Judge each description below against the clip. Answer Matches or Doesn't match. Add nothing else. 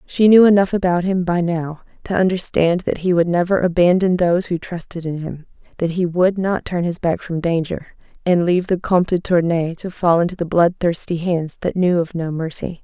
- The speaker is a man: Doesn't match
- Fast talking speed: Matches